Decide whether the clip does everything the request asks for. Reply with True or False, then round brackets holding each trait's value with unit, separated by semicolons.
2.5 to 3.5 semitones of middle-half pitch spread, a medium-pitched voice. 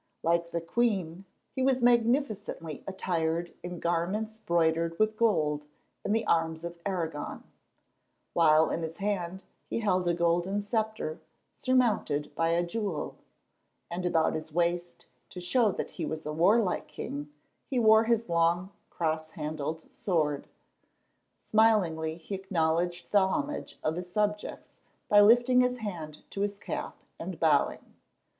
False (4.5 semitones; 175 Hz)